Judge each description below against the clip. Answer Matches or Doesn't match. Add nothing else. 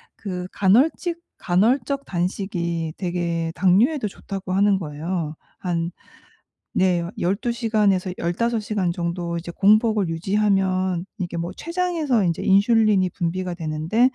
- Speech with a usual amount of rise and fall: Matches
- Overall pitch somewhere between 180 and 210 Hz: Matches